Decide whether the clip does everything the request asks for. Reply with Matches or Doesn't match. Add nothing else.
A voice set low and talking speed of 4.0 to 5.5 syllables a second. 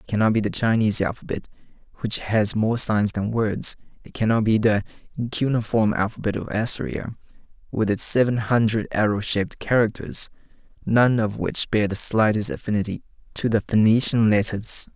Matches